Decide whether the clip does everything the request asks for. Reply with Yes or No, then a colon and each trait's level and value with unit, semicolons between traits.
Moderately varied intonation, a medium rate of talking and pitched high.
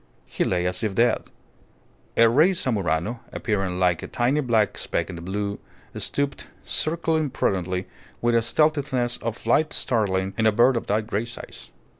No: average, 4.9 semitones; average, 165 wpm; low, 115 Hz